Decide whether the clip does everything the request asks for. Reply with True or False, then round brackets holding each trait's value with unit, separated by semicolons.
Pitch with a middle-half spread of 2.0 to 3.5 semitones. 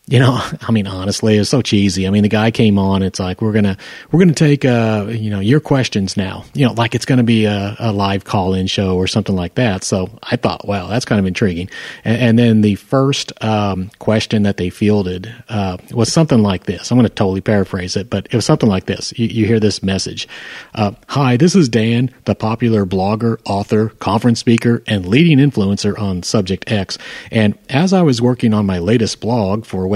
True (3.2 semitones)